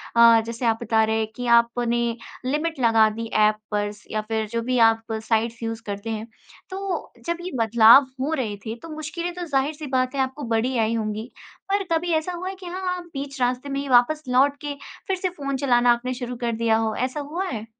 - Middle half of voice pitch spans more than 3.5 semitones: Yes, average, 4.5 semitones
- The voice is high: Yes, high, 245 Hz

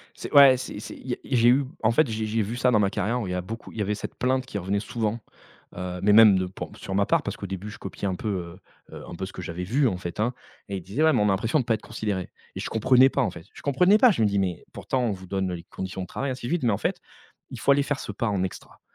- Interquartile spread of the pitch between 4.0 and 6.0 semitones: Yes, average, 4.6 semitones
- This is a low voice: Yes, low, 105 Hz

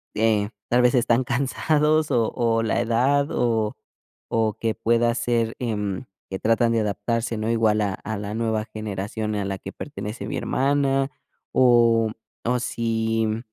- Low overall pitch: Yes, low, 115 Hz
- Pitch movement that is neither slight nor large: No, narrow, 2.0 semitones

